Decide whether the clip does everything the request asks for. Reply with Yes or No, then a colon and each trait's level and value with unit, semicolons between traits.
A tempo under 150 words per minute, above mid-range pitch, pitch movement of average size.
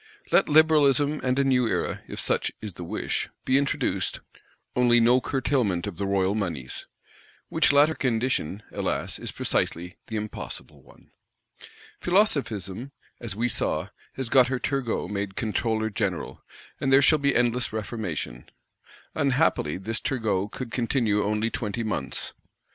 No: average, 140 wpm; low, 115 Hz; average, 4.7 semitones